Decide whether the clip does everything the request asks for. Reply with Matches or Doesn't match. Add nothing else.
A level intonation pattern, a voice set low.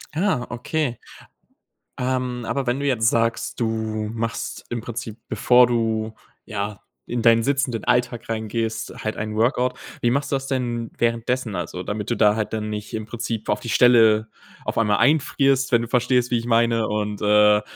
Matches